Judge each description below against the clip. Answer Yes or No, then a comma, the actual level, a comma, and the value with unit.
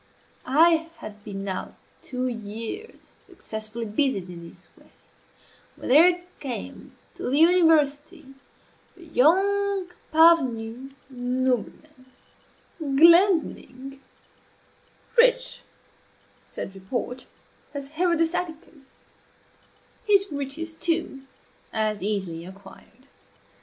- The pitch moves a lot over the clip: Yes, wide, 6.6 semitones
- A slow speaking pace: Yes, slow, 85 wpm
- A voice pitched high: Yes, very high, 275 Hz